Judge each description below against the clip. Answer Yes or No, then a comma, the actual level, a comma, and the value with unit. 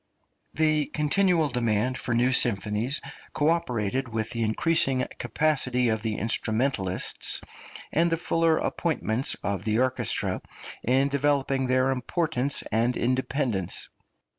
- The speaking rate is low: Yes, slow, 115 wpm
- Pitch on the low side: Yes, low, 130 Hz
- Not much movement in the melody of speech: No, average, 4.4 semitones